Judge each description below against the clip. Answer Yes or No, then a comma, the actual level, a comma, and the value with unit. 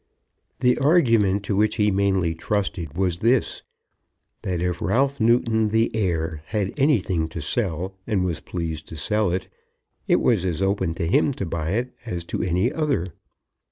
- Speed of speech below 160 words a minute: No, average, 165 wpm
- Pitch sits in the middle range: No, very low, 95 Hz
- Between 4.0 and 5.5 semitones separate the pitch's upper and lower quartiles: Yes, average, 4.7 semitones